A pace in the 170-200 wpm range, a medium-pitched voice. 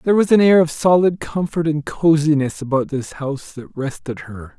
Yes: average, 195 wpm; medium, 155 Hz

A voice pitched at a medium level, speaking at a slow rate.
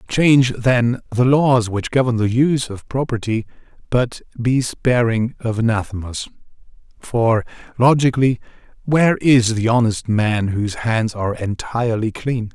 No: low, 120 Hz; slow, 130 wpm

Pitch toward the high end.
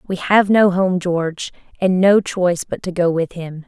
No: medium, 180 Hz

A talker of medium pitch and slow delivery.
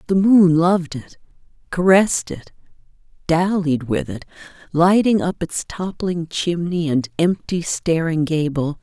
Yes: medium, 170 Hz; slow, 130 wpm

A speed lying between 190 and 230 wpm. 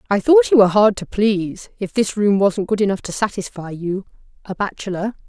Yes: fast, 205 wpm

